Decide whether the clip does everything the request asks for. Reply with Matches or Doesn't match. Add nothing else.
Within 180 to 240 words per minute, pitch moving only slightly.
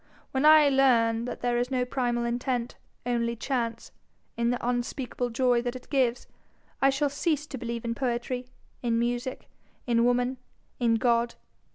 Doesn't match